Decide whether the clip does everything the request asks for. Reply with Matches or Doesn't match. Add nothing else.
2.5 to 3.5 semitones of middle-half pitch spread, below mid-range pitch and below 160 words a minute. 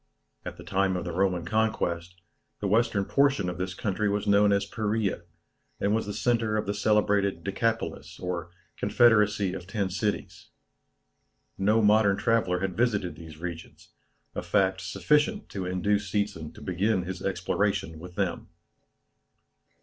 Matches